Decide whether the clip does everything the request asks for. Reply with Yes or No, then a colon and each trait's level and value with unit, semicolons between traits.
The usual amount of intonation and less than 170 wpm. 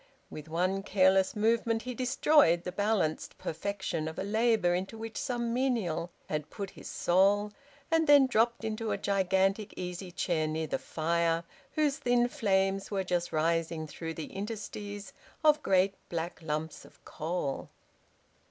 Yes: average, 4.9 semitones; average, 150 wpm